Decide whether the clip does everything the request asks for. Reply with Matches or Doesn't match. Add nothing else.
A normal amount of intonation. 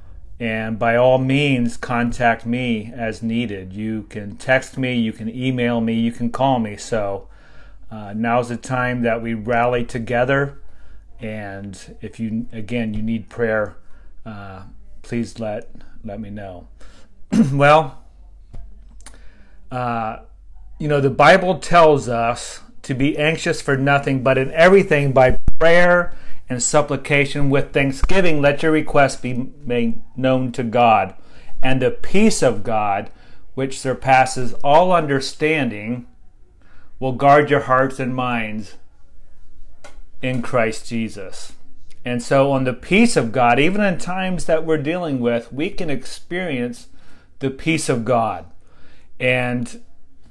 Matches